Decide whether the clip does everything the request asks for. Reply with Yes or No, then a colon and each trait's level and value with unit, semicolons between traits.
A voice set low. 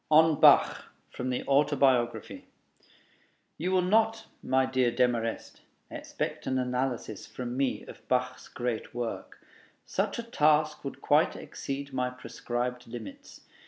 Yes: low, 130 Hz